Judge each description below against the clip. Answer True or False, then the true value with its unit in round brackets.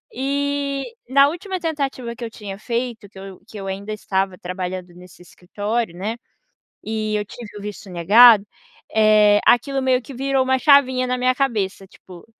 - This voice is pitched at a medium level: False (225 Hz)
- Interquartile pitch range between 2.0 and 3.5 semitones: False (5.0 semitones)